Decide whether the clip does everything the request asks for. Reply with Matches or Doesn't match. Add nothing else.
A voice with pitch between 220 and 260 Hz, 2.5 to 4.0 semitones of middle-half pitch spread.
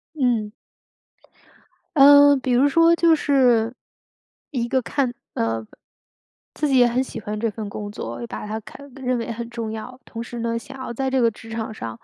Matches